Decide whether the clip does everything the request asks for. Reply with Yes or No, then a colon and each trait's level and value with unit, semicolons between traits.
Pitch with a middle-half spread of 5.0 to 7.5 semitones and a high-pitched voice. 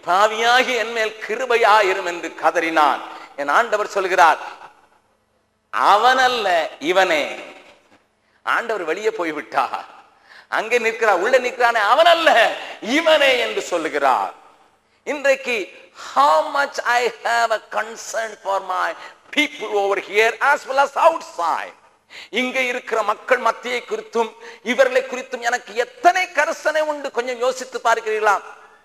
Yes: average, 5.3 semitones; high, 245 Hz